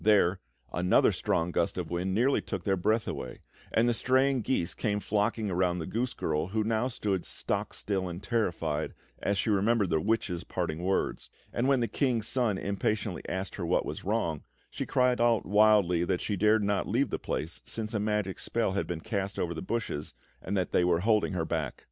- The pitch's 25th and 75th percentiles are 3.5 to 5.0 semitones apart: Yes, average, 4.1 semitones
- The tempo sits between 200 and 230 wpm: Yes, fast, 205 wpm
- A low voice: Yes, low, 100 Hz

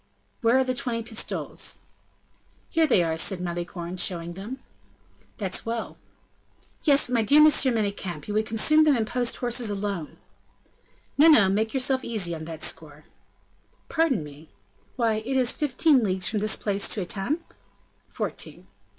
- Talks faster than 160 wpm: No, average, 155 wpm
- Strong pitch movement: Yes, wide, 5.8 semitones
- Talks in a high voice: Yes, high, 220 Hz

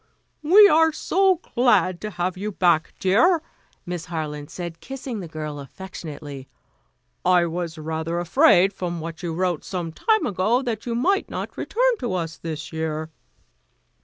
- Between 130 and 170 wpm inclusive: Yes, average, 155 wpm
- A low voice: No, medium, 180 Hz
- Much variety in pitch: Yes, wide, 7.0 semitones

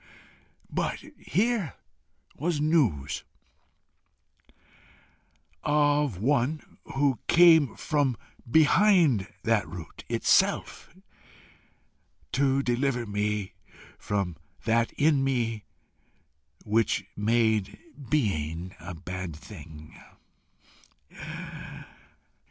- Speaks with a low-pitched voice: Yes, low, 120 Hz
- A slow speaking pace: Yes, slow, 70 wpm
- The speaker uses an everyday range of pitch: No, wide, 6.8 semitones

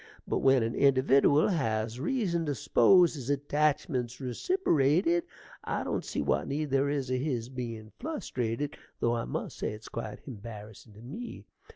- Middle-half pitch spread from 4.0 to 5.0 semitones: Yes, average, 4.4 semitones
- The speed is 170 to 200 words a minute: No, average, 160 wpm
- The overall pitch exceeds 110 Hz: Yes, low, 135 Hz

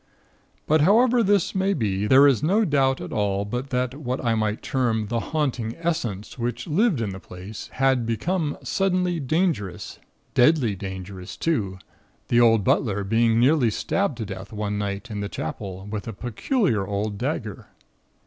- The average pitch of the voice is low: Yes, low, 120 Hz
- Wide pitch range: Yes, wide, 6.9 semitones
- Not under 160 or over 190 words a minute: Yes, average, 165 wpm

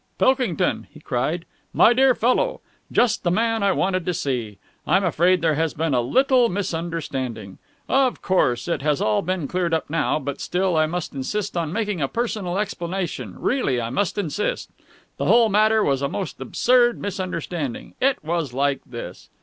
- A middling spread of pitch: No, wide, 6.6 semitones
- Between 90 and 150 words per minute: No, average, 175 wpm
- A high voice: No, medium, 175 Hz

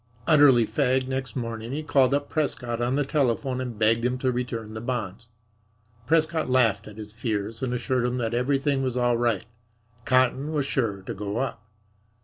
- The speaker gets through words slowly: No, average, 180 wpm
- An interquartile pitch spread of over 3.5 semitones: No, average, 2.7 semitones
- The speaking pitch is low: Yes, low, 125 Hz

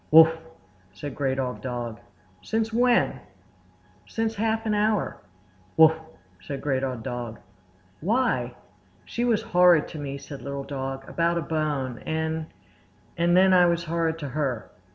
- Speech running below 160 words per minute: Yes, average, 140 wpm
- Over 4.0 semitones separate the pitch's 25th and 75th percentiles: Yes, average, 5.0 semitones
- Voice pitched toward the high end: No, medium, 160 Hz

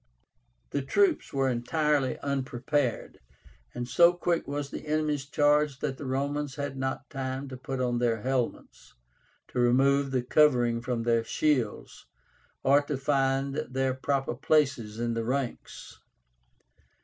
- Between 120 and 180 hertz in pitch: Yes, low, 135 Hz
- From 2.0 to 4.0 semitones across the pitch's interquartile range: Yes, narrow, 2.5 semitones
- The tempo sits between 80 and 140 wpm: Yes, slow, 135 wpm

